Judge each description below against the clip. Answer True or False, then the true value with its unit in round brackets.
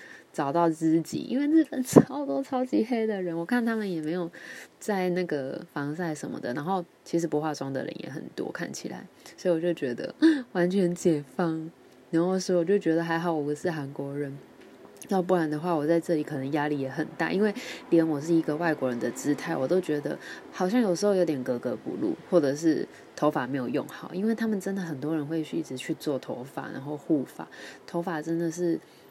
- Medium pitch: True (170 Hz)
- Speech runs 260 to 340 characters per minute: True (310 characters per minute)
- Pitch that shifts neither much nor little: True (4.0 semitones)